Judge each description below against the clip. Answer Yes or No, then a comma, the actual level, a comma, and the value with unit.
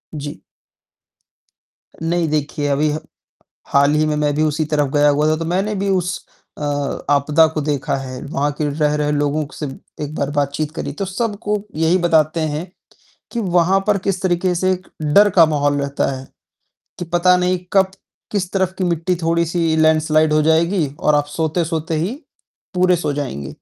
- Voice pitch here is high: No, medium, 160 Hz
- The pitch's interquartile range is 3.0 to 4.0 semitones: Yes, average, 3.3 semitones